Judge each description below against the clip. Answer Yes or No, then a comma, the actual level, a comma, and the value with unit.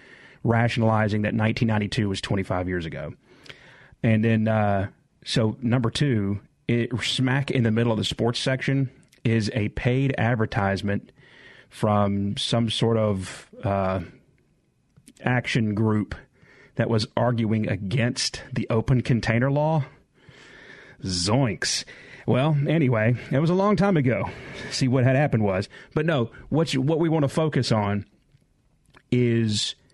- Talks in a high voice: No, low, 115 Hz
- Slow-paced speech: Yes, slow, 130 wpm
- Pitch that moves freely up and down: No, average, 3.8 semitones